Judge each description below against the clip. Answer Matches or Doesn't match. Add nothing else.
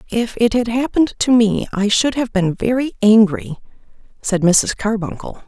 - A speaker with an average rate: Matches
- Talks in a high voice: Matches